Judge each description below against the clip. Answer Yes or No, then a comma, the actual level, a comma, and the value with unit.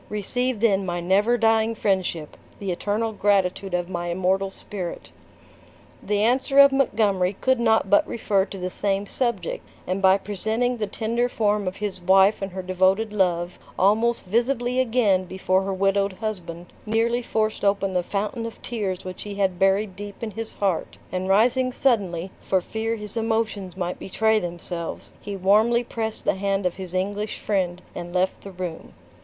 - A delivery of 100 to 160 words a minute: No, average, 170 wpm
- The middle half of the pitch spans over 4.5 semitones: No, average, 3.1 semitones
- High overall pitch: Yes, high, 200 Hz